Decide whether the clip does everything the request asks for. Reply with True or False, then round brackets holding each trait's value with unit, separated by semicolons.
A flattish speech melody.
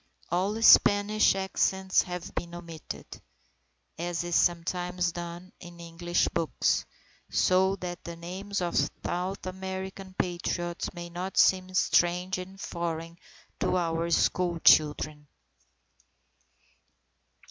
True (1.7 semitones)